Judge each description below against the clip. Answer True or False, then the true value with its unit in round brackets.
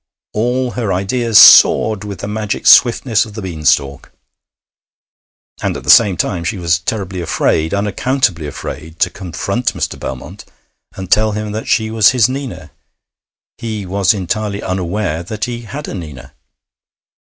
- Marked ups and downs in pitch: False (4.0 semitones)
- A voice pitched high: False (100 Hz)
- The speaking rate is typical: True (155 wpm)